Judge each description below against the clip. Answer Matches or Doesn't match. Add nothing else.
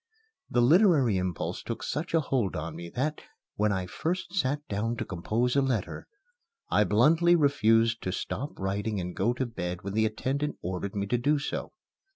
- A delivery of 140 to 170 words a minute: Doesn't match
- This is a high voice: Doesn't match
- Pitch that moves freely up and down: Matches